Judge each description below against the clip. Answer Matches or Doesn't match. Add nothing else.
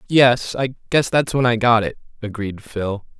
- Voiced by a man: Matches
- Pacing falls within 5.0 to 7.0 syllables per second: Doesn't match